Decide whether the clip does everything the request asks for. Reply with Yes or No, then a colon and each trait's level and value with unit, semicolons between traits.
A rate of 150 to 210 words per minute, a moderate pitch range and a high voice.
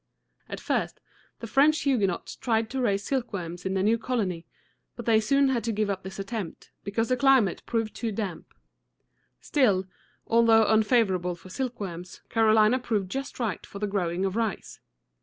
Yes: average, 165 wpm; average, 3.7 semitones; high, 220 Hz